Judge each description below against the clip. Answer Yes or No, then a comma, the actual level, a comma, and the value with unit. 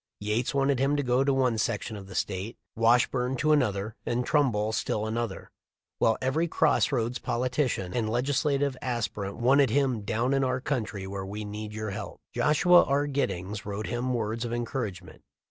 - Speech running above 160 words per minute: Yes, average, 175 wpm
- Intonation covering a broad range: No, average, 4.0 semitones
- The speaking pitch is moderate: No, low, 120 Hz